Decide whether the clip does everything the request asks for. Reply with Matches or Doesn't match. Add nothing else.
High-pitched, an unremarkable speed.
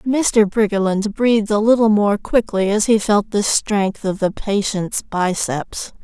Matches